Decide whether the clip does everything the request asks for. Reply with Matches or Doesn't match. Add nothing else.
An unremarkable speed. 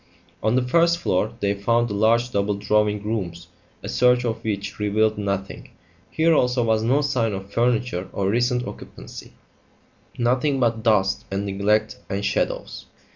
Matches